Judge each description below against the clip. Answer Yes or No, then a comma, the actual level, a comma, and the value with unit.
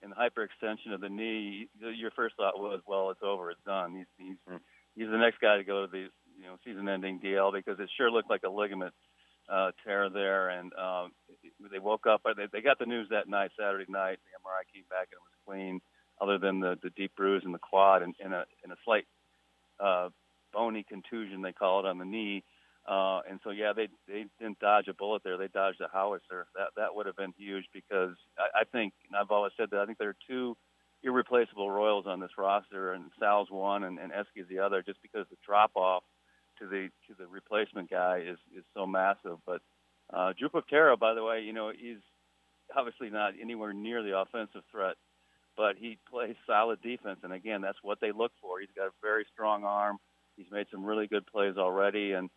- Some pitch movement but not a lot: No, narrow, 2.1 semitones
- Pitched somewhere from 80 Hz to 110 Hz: Yes, low, 100 Hz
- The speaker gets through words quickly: Yes, fast, 215 wpm